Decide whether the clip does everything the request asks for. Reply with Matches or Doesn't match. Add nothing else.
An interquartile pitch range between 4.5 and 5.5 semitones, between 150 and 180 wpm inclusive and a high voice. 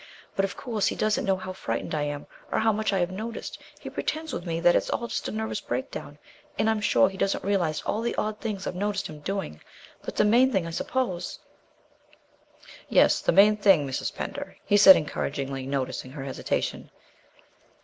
Doesn't match